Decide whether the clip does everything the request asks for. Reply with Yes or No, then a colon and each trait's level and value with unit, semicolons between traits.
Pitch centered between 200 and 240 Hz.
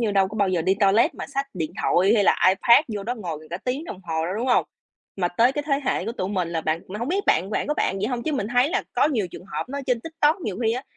Yes: high, 215 Hz